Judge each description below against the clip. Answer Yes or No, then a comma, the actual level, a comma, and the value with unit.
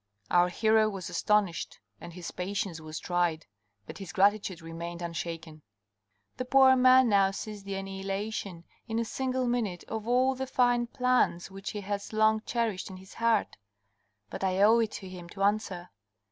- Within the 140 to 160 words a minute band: No, average, 170 wpm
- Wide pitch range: No, average, 4.1 semitones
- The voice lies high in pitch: Yes, high, 200 Hz